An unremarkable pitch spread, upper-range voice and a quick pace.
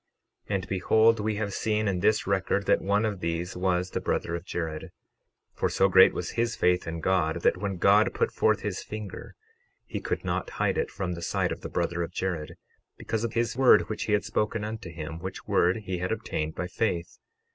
No: average, 3.6 semitones; very low, 95 Hz; fast, 215 wpm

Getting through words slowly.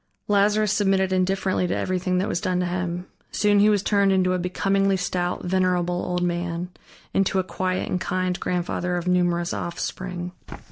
No: average, 170 wpm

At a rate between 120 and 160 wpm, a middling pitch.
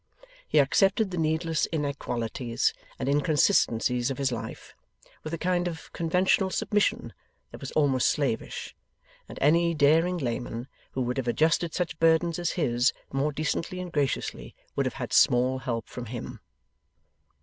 Yes: average, 150 wpm; medium, 150 Hz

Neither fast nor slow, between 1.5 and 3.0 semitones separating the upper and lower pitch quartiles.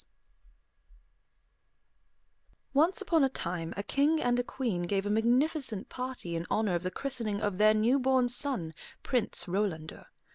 No: average, 150 wpm; wide, 5.5 semitones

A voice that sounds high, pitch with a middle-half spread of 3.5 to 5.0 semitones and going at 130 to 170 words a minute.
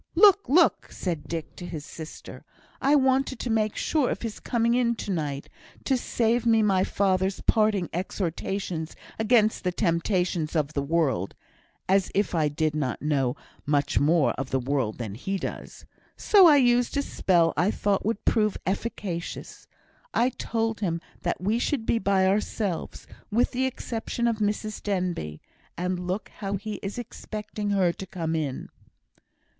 No: high, 195 Hz; wide, 5.5 semitones; average, 160 wpm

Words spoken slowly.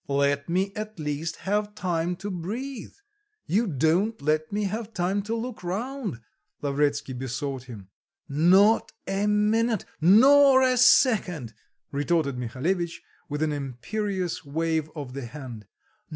Yes: slow, 130 wpm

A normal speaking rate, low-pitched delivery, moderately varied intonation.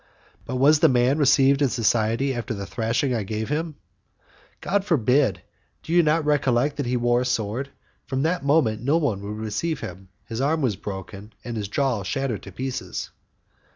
Yes: average, 185 wpm; low, 125 Hz; average, 4.7 semitones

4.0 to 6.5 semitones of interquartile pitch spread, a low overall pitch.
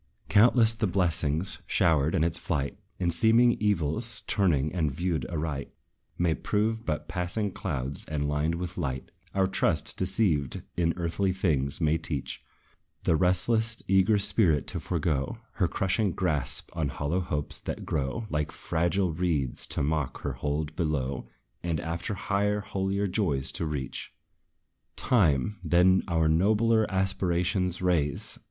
Yes: average, 4.4 semitones; very low, 85 Hz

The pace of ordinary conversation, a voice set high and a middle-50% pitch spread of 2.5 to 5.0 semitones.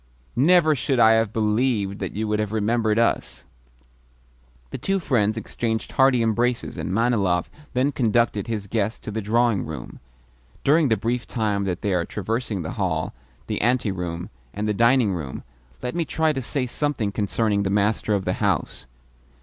No: average, 170 wpm; low, 110 Hz; average, 3.3 semitones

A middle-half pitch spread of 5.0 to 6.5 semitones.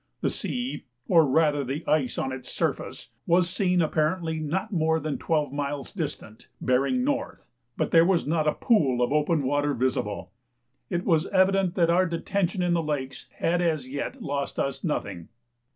No: average, 4.1 semitones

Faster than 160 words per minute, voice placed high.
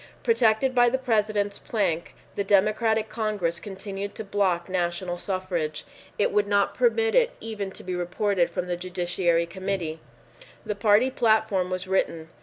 No: average, 150 wpm; high, 200 Hz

